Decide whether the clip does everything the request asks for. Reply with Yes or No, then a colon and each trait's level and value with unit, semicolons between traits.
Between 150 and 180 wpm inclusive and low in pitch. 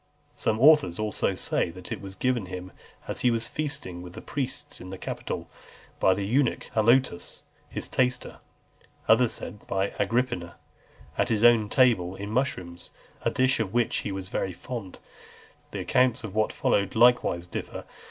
Yes: average, 165 wpm; low, 110 Hz